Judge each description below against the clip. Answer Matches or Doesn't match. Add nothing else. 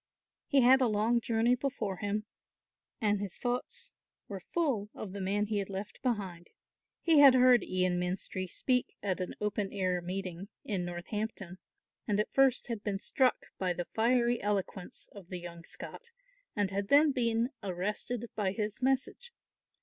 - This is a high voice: Matches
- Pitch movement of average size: Matches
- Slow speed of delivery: Doesn't match